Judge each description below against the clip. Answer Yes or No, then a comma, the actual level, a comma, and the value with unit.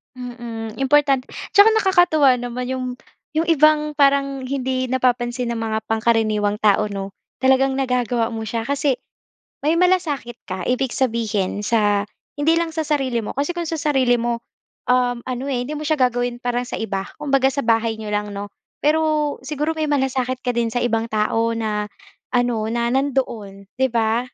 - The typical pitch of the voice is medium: No, very high, 250 Hz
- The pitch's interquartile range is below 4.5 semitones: Yes, average, 3.7 semitones